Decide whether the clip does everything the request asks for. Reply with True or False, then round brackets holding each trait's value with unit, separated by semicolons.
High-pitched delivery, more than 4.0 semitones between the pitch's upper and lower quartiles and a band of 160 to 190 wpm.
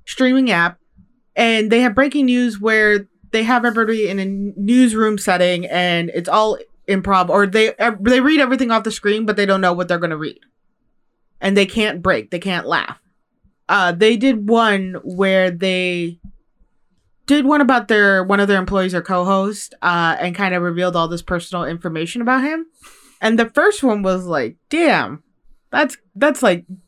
True (200 Hz; 4.8 semitones; 180 wpm)